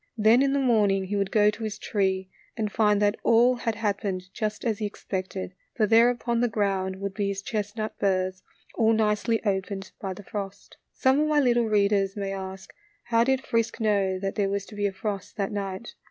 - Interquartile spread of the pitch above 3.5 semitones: No, narrow, 2.5 semitones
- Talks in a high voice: Yes, high, 205 Hz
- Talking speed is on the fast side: Yes, fast, 210 wpm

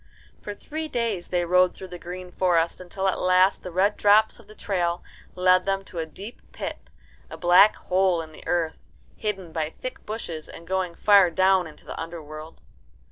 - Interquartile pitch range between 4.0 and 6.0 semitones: No, narrow, 2.5 semitones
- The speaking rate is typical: Yes, average, 190 wpm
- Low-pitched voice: No, medium, 185 Hz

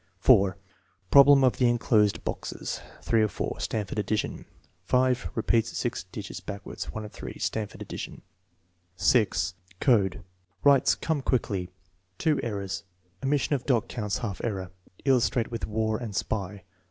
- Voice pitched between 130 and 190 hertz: No, low, 110 Hz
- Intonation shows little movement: No, average, 3.8 semitones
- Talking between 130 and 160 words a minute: Yes, average, 140 wpm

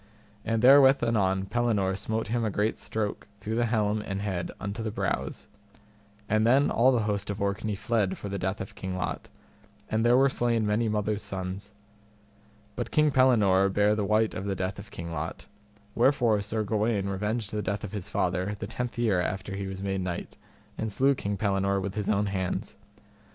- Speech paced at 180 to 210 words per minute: Yes, average, 195 wpm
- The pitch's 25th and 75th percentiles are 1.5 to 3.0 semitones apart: Yes, narrow, 2.5 semitones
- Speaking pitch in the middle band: No, low, 105 Hz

